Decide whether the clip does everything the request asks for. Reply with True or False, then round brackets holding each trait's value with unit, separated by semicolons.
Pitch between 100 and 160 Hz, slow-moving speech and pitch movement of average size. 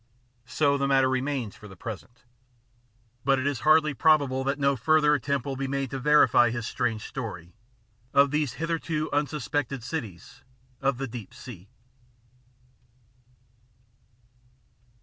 True (135 Hz; 130 wpm; 3.4 semitones)